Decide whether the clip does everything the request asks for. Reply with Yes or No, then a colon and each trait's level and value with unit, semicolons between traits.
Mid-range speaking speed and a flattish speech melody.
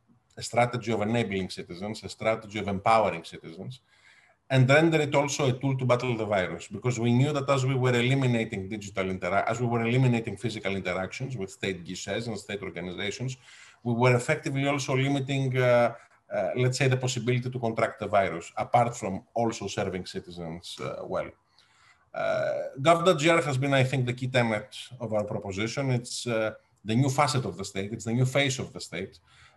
No: average, 185 wpm; average, 3.7 semitones